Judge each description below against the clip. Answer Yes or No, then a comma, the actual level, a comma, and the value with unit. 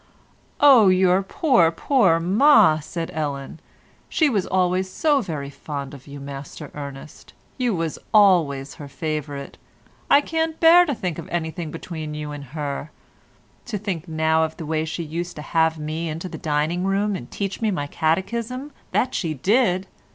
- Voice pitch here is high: No, medium, 165 Hz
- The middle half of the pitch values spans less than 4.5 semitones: No, average, 4.8 semitones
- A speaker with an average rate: Yes, average, 165 wpm